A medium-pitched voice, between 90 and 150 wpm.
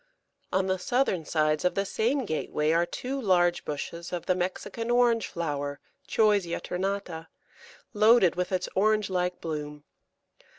Yes: medium, 180 Hz; average, 140 wpm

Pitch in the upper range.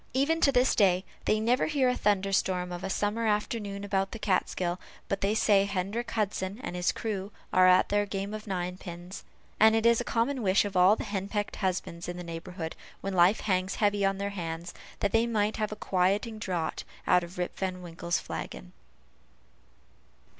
Yes: high, 195 Hz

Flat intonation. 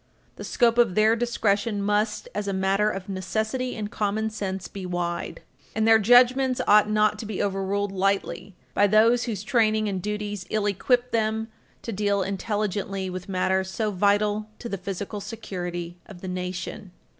Yes: narrow, 2.2 semitones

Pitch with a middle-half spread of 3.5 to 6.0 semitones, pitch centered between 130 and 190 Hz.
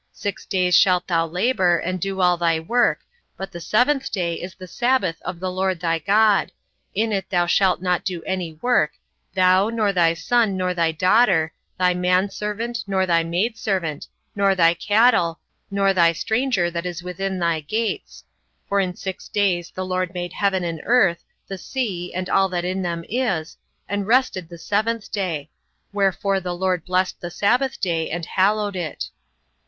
No: average, 2.7 semitones; medium, 185 Hz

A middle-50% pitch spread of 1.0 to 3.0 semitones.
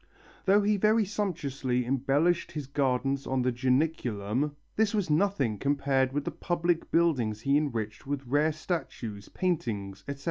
No: average, 5.1 semitones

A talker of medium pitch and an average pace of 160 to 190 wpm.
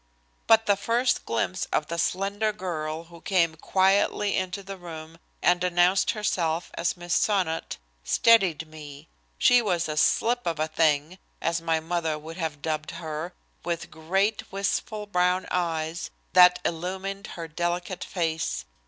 No: medium, 175 Hz; average, 145 wpm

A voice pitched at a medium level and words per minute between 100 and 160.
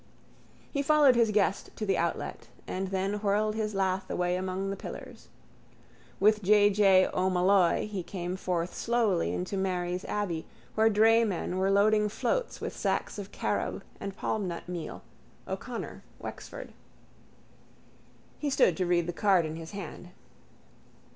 No: high, 195 Hz; average, 140 wpm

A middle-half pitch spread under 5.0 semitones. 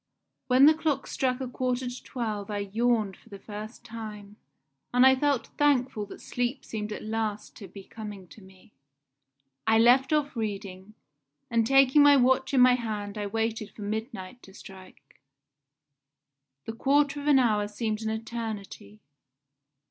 Yes: average, 3.6 semitones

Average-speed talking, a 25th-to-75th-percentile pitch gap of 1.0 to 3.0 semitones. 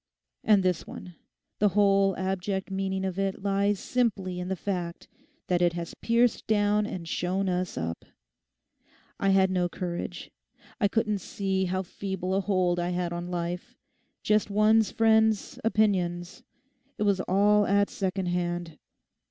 Yes: average, 145 wpm; narrow, 2.4 semitones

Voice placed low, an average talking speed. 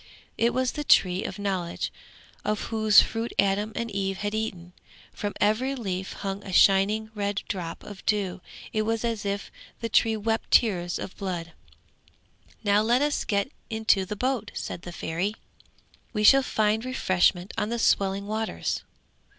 No: high, 210 Hz; average, 160 wpm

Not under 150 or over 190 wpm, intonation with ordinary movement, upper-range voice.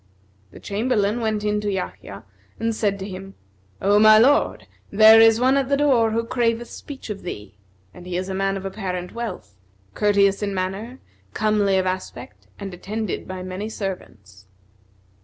Yes: average, 170 wpm; average, 3.1 semitones; high, 205 Hz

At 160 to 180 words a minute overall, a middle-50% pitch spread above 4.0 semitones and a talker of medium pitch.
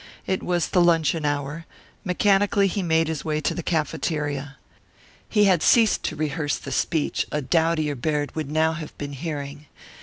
No: average, 170 wpm; average, 2.9 semitones; medium, 155 Hz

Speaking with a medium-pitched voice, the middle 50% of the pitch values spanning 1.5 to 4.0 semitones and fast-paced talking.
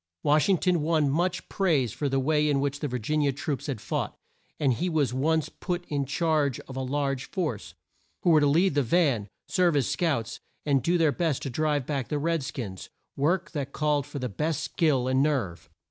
Yes: medium, 145 Hz; average, 3.2 semitones; fast, 225 wpm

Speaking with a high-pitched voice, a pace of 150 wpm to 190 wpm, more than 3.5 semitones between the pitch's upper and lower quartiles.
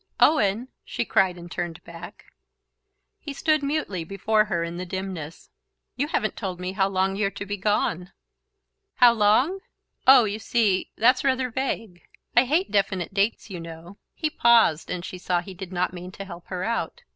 Yes: high, 195 Hz; average, 175 wpm; average, 4.7 semitones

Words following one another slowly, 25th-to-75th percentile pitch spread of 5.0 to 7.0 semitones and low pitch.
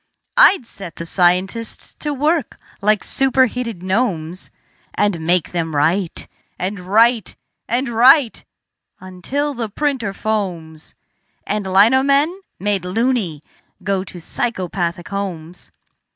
No: slow, 110 wpm; wide, 5.4 semitones; high, 200 Hz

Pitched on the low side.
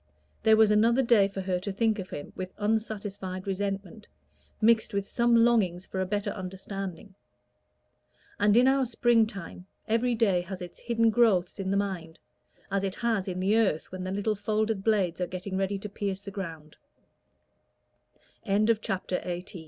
No: high, 200 Hz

